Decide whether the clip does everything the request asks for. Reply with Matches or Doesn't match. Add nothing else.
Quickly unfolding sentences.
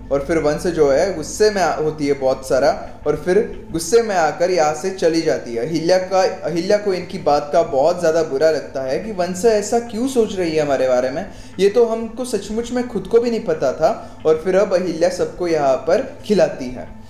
Matches